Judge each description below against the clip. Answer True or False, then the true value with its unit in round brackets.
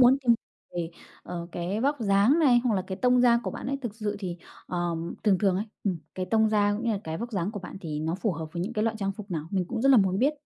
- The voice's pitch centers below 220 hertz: True (205 Hz)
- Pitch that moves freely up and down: False (4.5 semitones)